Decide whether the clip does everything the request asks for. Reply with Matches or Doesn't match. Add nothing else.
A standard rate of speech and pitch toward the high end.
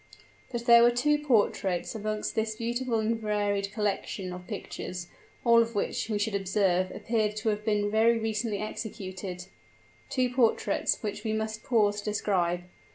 Matches